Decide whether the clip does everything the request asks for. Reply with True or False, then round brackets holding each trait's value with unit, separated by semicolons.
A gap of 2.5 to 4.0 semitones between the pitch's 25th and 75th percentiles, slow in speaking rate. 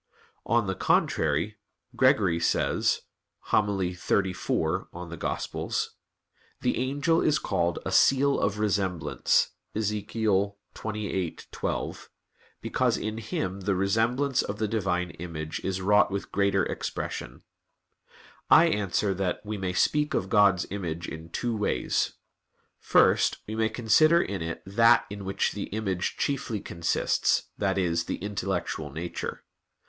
True (3.3 semitones; 125 wpm)